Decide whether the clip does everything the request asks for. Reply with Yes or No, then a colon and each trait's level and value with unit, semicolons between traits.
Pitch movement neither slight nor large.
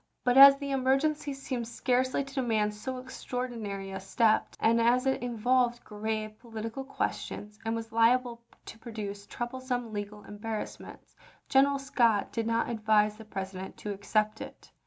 Yes: average, 3.2 semitones